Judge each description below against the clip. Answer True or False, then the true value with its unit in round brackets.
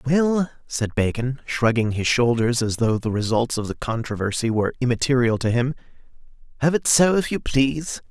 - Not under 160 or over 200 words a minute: True (170 wpm)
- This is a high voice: False (125 Hz)